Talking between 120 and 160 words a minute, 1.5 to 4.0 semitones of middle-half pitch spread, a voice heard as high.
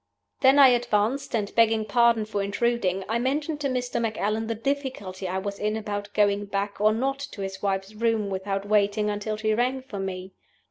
No: average, 190 wpm; average, 2.9 semitones; high, 215 Hz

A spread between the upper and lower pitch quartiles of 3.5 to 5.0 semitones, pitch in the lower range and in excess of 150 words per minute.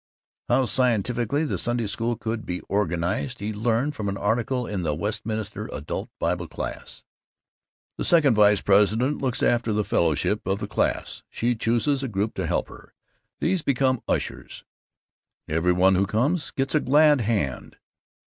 Yes: average, 4.3 semitones; low, 110 Hz; average, 160 wpm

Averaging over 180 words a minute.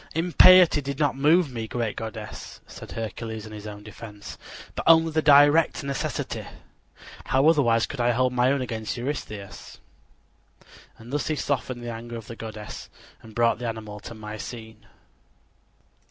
No: average, 155 wpm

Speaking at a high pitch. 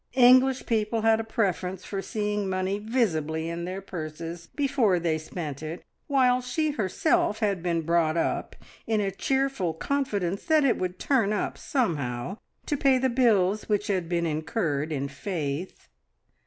Yes: high, 195 Hz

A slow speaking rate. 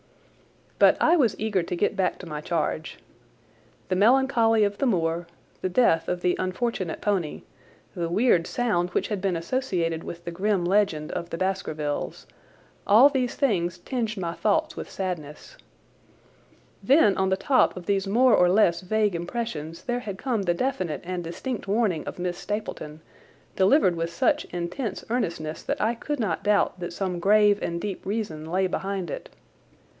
No: average, 170 wpm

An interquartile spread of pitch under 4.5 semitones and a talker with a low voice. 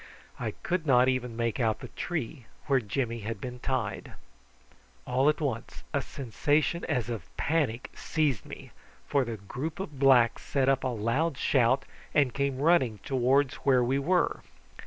Yes: average, 3.5 semitones; low, 130 Hz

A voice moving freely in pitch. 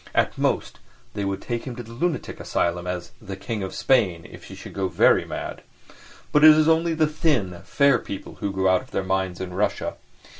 Yes: wide, 7.1 semitones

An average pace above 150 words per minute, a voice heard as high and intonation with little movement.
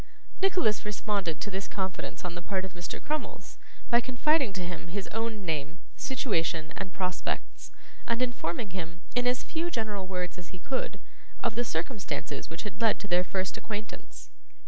No: average, 170 wpm; high, 195 Hz; average, 4.8 semitones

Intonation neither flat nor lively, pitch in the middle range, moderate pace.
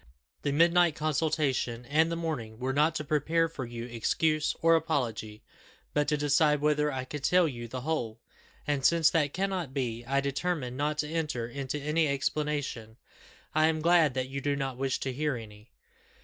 Yes: average, 3.5 semitones; medium, 145 Hz; average, 180 wpm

